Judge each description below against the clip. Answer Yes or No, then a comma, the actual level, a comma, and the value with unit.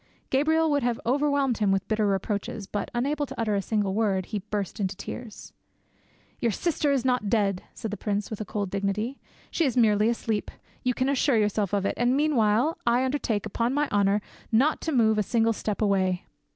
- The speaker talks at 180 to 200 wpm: Yes, average, 195 wpm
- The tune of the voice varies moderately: Yes, average, 4.1 semitones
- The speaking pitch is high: Yes, high, 220 Hz